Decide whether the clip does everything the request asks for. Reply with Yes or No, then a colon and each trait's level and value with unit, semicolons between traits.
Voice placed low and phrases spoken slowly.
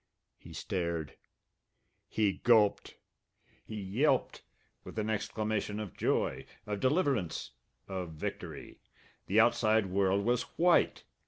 Yes: low, 105 Hz; slow, 105 wpm